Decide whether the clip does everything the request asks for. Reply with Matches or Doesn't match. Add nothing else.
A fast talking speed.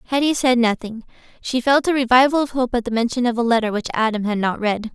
Matches